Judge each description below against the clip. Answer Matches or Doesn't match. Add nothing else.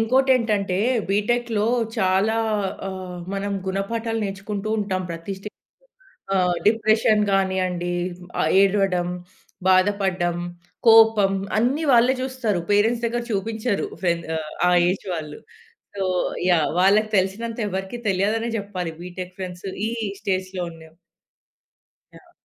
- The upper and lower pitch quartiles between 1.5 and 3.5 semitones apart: Matches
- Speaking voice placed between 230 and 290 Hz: Doesn't match